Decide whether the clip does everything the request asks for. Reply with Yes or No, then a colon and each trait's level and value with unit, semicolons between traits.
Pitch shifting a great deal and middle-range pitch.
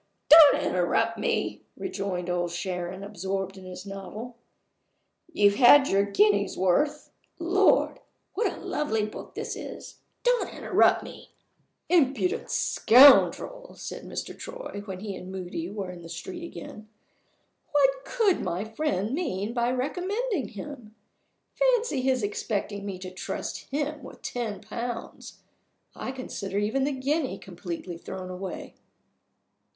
No: wide, 7.5 semitones; high, 220 Hz